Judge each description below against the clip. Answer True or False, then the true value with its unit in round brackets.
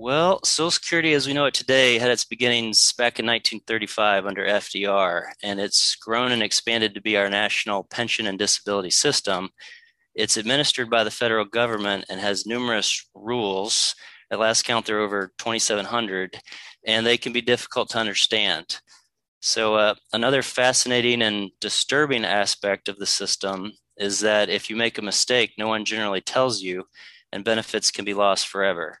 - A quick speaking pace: False (170 wpm)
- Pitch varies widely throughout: False (3.0 semitones)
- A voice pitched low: True (110 Hz)